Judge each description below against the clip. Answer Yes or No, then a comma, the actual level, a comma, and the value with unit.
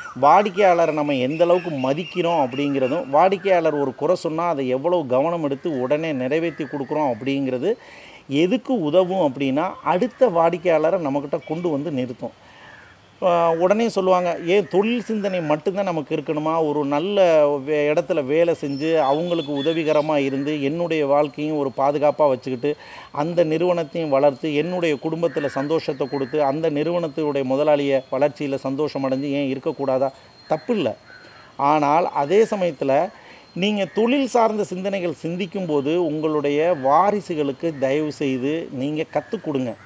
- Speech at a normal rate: Yes, average, 120 wpm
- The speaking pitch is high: No, medium, 155 Hz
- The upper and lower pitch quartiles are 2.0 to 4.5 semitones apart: Yes, average, 3.6 semitones